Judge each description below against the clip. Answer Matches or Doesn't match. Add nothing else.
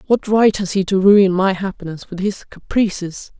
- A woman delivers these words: Matches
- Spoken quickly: Doesn't match